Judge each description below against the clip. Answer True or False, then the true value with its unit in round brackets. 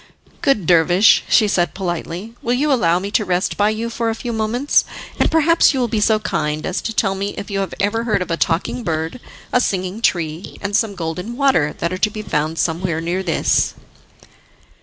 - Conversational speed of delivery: False (210 wpm)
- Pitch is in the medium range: False (200 Hz)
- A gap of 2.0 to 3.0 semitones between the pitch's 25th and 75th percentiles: False (4.7 semitones)